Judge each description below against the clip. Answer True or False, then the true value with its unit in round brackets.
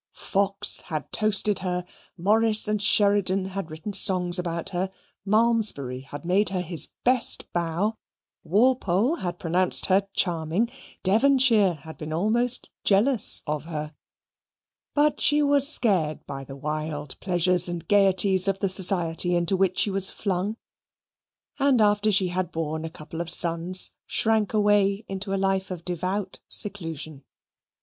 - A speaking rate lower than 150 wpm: True (140 wpm)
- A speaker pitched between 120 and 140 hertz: False (190 Hz)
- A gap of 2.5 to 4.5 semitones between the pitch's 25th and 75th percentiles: True (3.6 semitones)